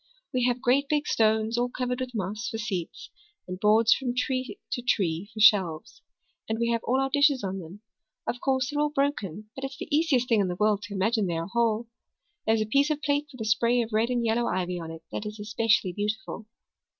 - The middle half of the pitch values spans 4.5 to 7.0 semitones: No, average, 3.5 semitones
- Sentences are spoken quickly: Yes, fast, 235 wpm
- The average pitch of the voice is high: Yes, high, 225 Hz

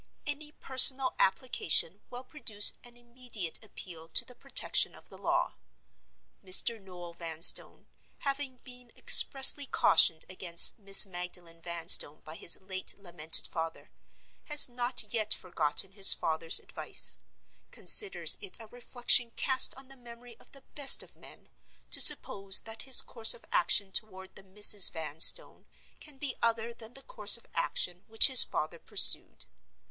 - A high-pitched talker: Yes, high, 215 Hz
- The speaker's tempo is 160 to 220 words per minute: No, average, 145 wpm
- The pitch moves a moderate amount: No, wide, 6.0 semitones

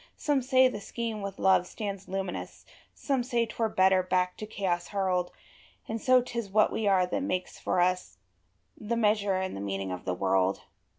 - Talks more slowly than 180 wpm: No, average, 195 wpm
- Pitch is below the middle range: No, high, 195 Hz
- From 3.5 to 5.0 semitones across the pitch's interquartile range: Yes, average, 3.9 semitones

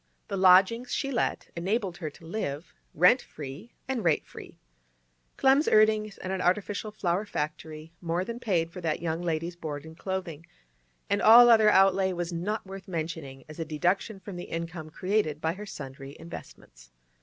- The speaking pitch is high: No, medium, 180 Hz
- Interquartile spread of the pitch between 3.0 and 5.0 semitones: Yes, average, 4.1 semitones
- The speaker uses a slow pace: No, average, 170 wpm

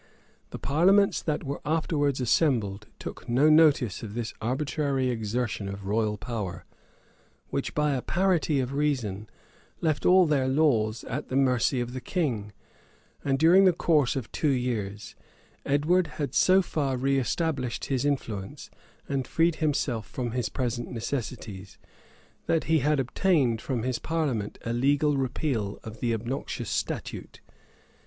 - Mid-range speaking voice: No, low, 130 Hz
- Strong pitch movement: No, average, 4.5 semitones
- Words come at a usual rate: Yes, average, 145 wpm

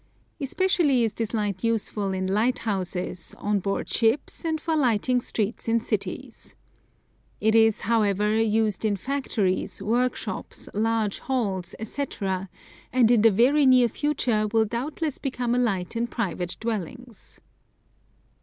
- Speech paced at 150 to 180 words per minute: No, slow, 135 wpm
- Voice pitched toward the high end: Yes, high, 225 Hz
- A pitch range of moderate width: Yes, average, 3.4 semitones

